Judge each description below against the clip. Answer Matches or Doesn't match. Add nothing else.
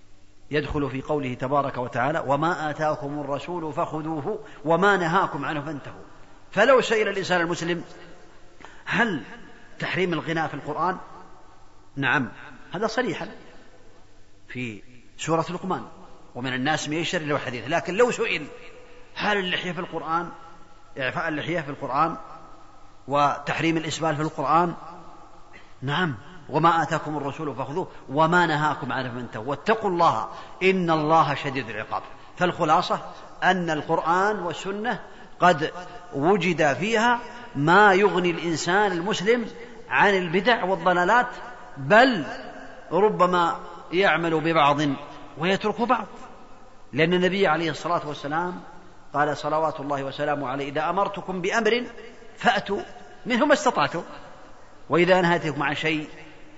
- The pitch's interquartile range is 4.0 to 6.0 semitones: Matches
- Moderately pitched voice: Matches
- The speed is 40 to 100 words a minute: Doesn't match